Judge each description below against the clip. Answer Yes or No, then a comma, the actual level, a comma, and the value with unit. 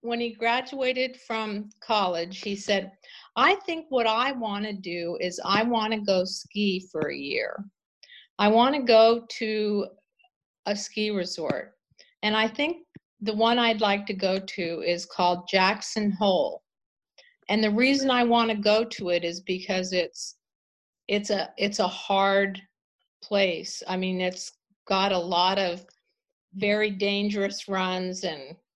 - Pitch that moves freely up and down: No, average, 3.3 semitones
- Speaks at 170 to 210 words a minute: No, average, 155 wpm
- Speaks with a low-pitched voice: No, high, 205 Hz